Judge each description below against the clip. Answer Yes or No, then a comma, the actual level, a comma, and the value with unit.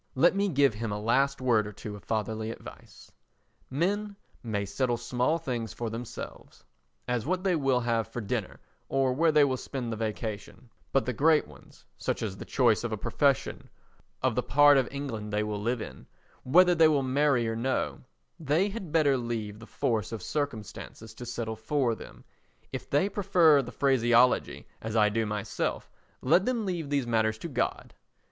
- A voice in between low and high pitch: No, low, 125 Hz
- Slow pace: No, average, 175 wpm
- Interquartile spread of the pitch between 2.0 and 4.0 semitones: No, average, 4.7 semitones